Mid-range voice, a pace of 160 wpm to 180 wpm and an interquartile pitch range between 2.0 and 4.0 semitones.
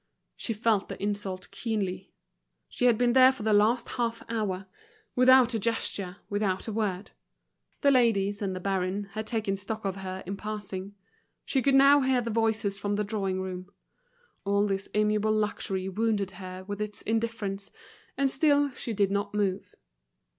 No: high, 210 Hz; average, 170 wpm; average, 2.8 semitones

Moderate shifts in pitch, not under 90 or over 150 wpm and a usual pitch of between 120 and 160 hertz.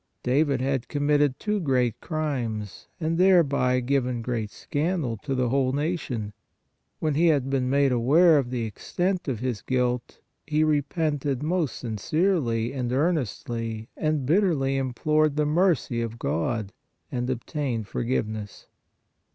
Yes: average, 4.2 semitones; average, 140 wpm; low, 135 Hz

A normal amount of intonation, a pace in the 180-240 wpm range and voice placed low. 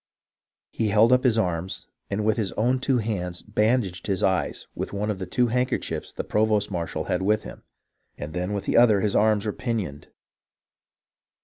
Yes: average, 3.1 semitones; average, 185 wpm; low, 105 Hz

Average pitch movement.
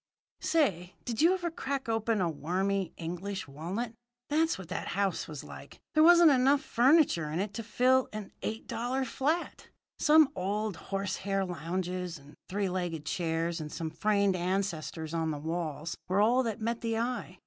No: wide, 6.0 semitones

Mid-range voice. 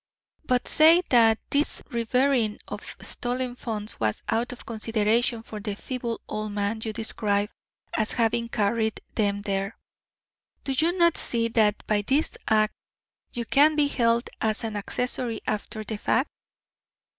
No: high, 225 Hz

